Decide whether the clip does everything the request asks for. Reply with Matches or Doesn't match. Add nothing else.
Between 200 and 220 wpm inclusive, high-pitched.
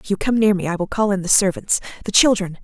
Doesn't match